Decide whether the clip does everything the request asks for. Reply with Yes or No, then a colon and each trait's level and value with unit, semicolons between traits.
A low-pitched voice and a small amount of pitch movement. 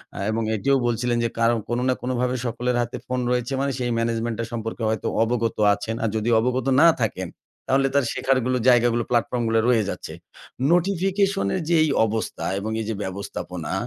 Yes: low, 120 Hz; narrow, 2.2 semitones